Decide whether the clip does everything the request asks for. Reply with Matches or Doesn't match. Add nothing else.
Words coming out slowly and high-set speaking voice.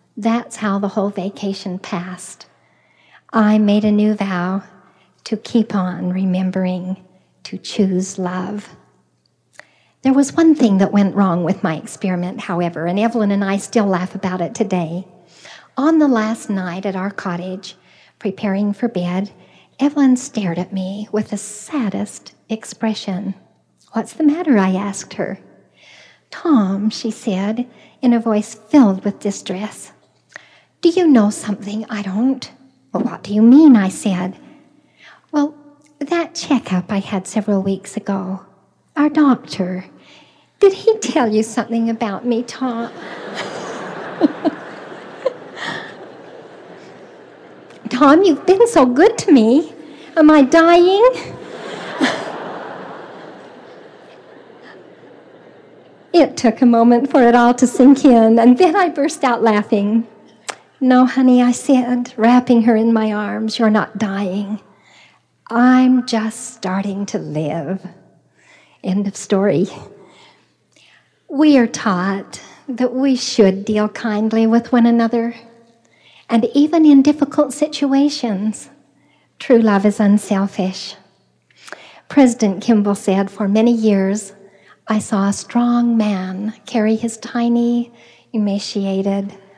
Matches